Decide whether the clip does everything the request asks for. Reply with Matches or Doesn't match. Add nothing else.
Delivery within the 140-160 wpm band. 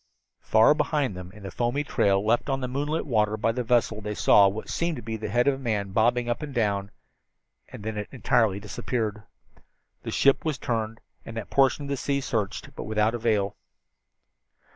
Doesn't match